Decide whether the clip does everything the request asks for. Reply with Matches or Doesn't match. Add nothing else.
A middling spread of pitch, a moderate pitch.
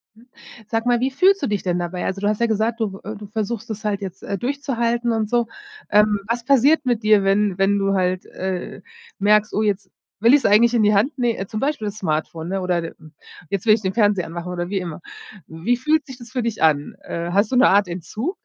Doesn't match